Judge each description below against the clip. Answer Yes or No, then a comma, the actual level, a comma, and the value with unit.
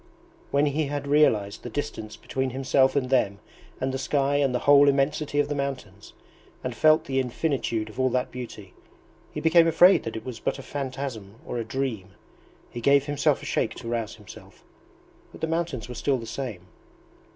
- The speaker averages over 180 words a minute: Yes, average, 190 wpm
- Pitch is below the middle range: Yes, low, 130 Hz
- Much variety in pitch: No, average, 3.8 semitones